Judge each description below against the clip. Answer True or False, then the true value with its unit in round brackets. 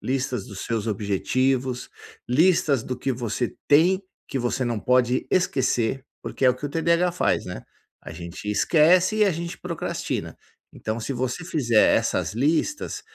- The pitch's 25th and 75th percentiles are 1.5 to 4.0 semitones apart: False (5.6 semitones)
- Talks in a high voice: False (130 Hz)